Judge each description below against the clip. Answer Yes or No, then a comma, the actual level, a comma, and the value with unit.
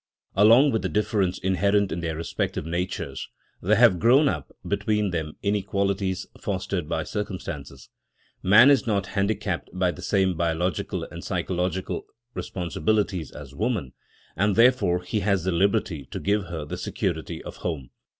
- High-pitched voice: No, very low, 95 Hz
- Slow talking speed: No, average, 150 wpm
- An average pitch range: Yes, average, 3.4 semitones